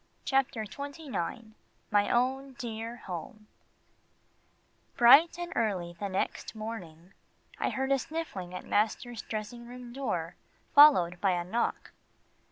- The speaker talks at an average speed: No, slow, 120 wpm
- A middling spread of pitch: No, wide, 5.7 semitones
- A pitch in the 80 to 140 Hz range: No, high, 230 Hz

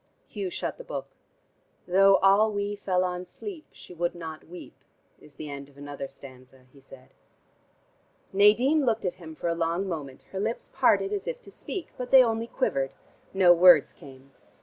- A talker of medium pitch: Yes, medium, 180 Hz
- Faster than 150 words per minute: Yes, average, 180 wpm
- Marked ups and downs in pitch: Yes, wide, 7.0 semitones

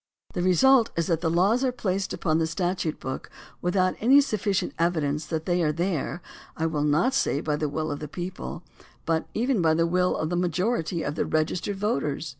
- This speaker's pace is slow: No, fast, 205 wpm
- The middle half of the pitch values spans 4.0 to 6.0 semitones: No, average, 3.5 semitones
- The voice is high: No, medium, 175 Hz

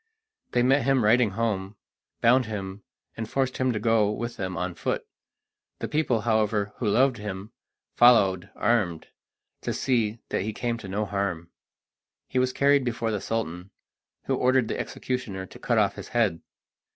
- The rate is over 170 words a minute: No, average, 165 wpm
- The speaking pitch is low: Yes, low, 110 Hz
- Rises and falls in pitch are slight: No, average, 3.6 semitones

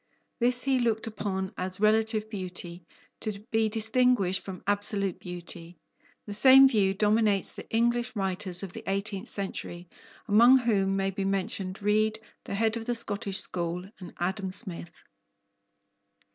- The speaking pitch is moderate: No, high, 200 Hz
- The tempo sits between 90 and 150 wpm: Yes, average, 145 wpm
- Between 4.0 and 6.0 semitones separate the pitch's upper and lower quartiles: No, average, 2.9 semitones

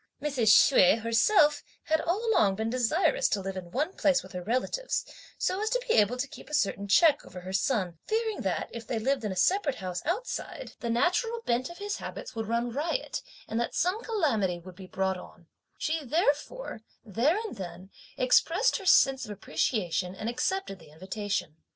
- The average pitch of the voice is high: Yes, high, 245 Hz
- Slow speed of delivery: No, average, 195 wpm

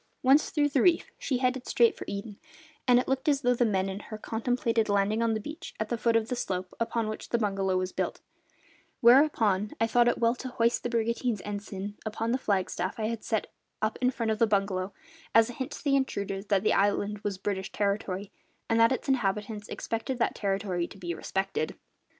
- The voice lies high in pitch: Yes, high, 220 Hz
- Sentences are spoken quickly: Yes, fast, 215 wpm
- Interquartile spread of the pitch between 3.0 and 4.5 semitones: Yes, average, 3.3 semitones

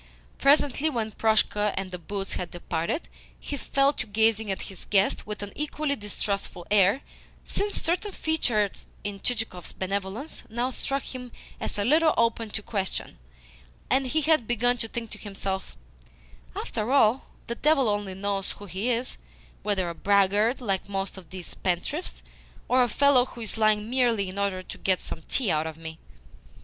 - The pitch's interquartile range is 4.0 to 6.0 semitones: Yes, average, 4.5 semitones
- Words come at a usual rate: Yes, average, 170 wpm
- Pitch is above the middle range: Yes, high, 215 Hz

